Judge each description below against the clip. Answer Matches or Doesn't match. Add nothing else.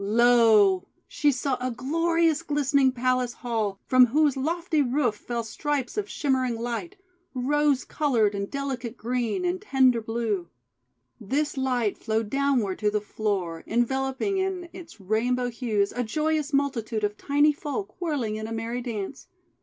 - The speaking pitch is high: Matches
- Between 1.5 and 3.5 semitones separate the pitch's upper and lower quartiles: Doesn't match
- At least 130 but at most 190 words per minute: Matches